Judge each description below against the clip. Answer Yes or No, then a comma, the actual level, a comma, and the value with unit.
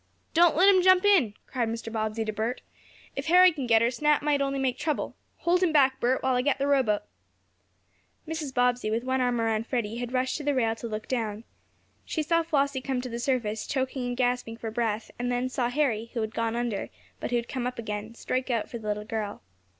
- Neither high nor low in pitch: No, high, 245 Hz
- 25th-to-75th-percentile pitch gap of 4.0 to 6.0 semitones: No, average, 3.5 semitones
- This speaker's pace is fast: Yes, fast, 230 wpm